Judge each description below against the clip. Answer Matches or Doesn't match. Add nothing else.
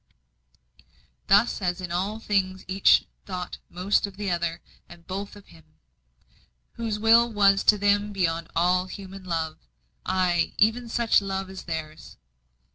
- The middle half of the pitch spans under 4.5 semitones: Matches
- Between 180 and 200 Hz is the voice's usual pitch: Matches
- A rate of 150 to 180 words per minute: Doesn't match